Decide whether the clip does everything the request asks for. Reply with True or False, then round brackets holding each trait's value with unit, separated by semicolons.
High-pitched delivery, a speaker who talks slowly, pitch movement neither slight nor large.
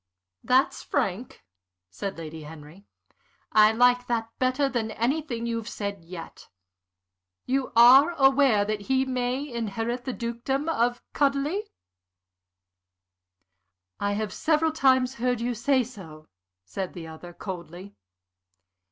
True (235 Hz; 115 wpm; 4.7 semitones)